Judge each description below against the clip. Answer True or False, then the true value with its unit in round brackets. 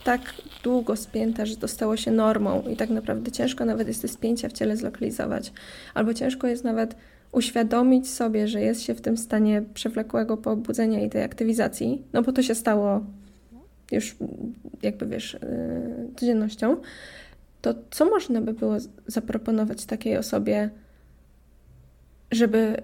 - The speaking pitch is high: True (225 Hz)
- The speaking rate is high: False (145 wpm)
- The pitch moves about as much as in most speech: True (3.2 semitones)